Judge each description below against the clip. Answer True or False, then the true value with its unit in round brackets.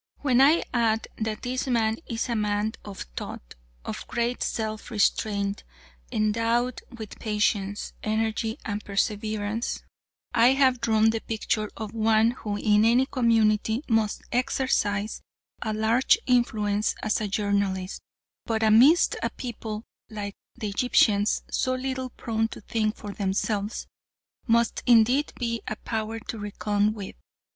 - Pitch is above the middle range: True (220 Hz)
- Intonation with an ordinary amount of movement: False (2.1 semitones)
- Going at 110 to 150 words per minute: True (135 wpm)